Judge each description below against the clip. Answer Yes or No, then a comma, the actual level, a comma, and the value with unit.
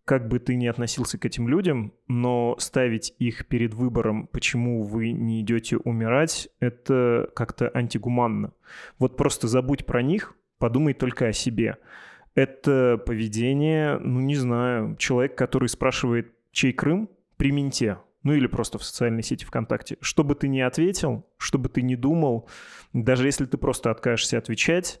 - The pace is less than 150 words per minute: No, average, 155 wpm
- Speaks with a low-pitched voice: Yes, low, 125 Hz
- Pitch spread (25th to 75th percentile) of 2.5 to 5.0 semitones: Yes, average, 2.8 semitones